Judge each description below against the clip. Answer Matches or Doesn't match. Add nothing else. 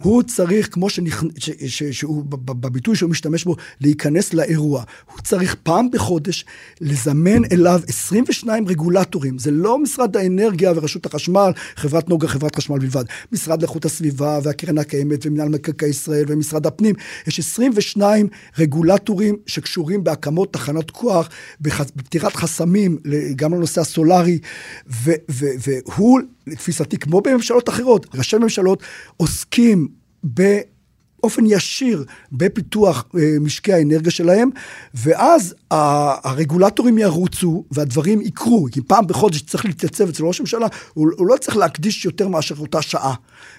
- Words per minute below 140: Matches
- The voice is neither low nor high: Matches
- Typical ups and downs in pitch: Matches